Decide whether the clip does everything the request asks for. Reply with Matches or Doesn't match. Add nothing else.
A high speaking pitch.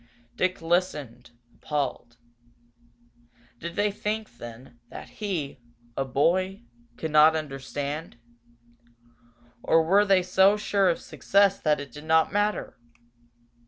Doesn't match